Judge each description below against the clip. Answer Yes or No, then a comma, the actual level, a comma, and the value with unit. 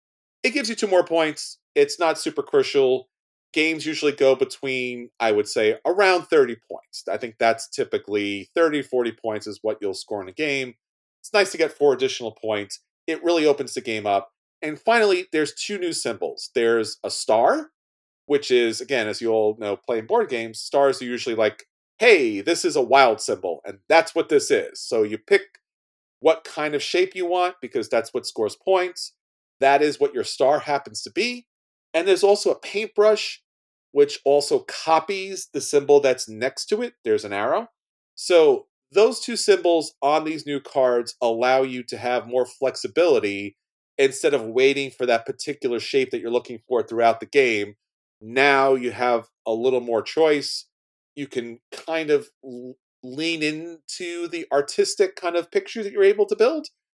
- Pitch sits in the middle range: Yes, medium, 165 Hz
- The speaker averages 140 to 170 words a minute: No, average, 180 wpm